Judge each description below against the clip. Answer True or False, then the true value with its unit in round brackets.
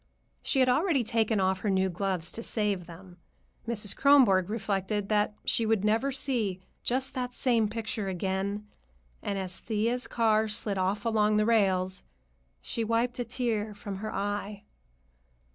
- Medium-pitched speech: False (210 Hz)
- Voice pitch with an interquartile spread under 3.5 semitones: True (2.9 semitones)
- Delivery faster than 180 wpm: False (155 wpm)